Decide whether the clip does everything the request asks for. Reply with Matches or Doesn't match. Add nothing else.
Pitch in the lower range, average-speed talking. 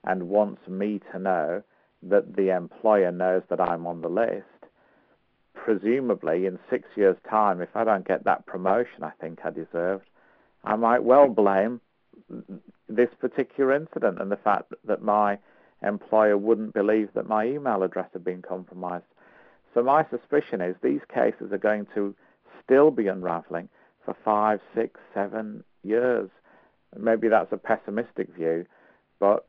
Matches